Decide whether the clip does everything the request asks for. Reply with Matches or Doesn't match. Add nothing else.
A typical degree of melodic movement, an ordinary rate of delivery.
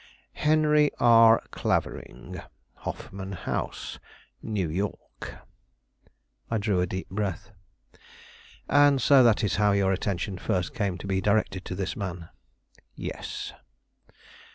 Doesn't match